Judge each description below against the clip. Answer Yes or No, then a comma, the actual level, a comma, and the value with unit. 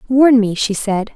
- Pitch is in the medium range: No, high, 225 Hz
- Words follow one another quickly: Yes, fast, 210 wpm